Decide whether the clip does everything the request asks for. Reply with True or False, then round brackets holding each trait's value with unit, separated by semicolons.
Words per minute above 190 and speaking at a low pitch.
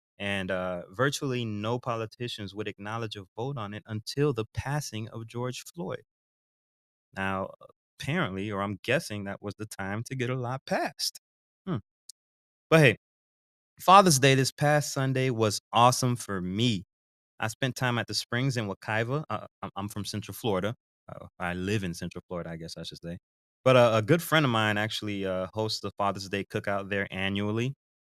False (180 wpm; 105 Hz)